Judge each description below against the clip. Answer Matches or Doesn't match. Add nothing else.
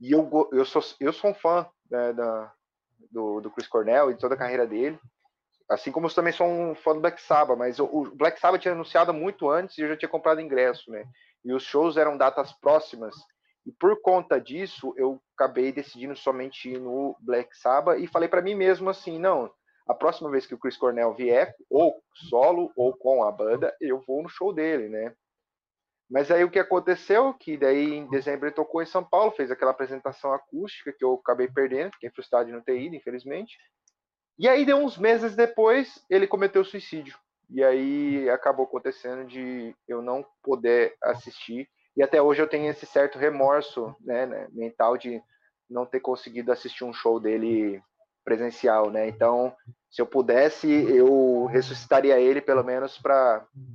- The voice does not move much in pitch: Doesn't match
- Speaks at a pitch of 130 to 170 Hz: Matches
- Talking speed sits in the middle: Doesn't match